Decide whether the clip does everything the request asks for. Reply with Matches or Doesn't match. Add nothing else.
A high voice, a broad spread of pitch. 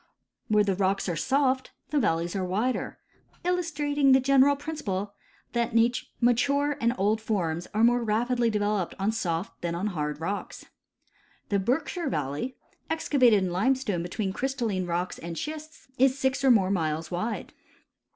Matches